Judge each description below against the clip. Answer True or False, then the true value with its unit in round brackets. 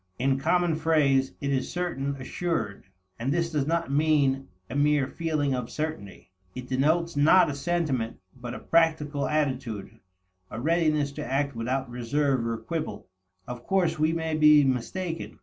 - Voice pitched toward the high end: False (145 Hz)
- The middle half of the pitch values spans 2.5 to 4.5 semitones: True (3.5 semitones)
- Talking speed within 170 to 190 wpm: False (155 wpm)